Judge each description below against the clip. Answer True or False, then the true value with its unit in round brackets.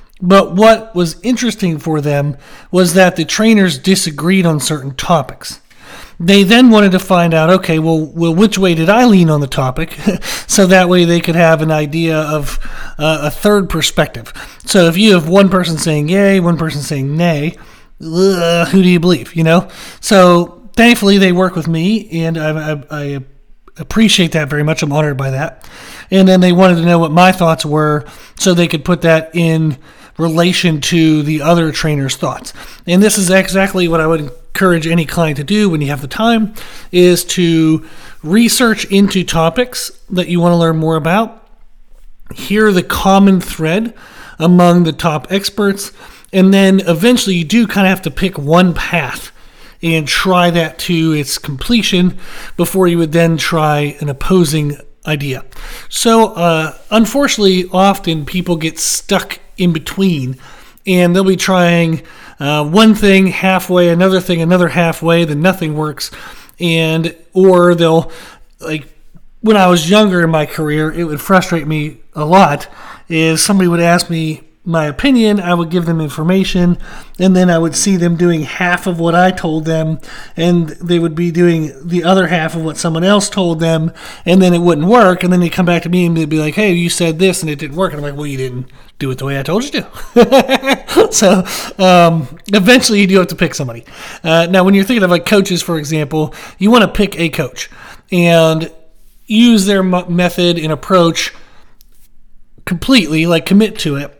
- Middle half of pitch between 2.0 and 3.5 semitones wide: True (3.0 semitones)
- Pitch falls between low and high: True (175 Hz)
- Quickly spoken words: False (185 wpm)